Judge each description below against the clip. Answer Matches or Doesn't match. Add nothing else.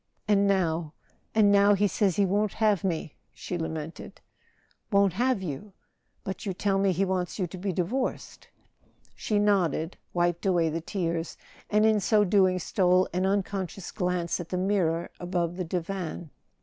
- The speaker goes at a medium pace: Matches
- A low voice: Doesn't match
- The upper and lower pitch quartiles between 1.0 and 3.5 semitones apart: Matches